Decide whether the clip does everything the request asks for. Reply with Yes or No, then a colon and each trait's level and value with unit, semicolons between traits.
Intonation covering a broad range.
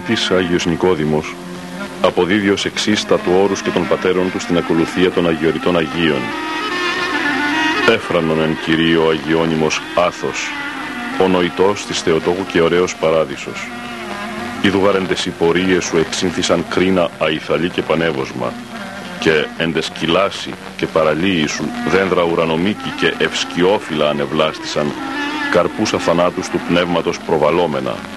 No: average, 2.7 semitones